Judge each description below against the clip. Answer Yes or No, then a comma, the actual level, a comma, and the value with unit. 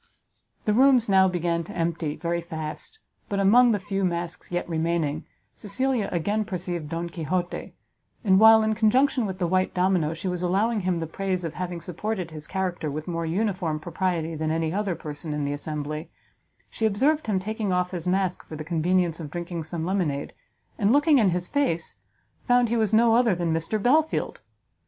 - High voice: No, medium, 180 Hz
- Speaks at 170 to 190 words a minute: Yes, average, 185 wpm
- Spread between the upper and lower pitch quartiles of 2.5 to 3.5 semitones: No, average, 4.2 semitones